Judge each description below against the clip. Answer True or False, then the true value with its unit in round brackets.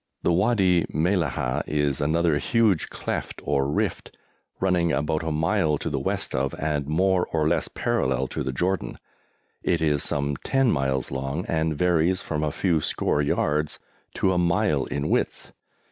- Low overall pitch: True (80 Hz)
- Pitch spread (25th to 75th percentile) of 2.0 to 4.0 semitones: True (3.6 semitones)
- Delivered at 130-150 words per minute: False (160 wpm)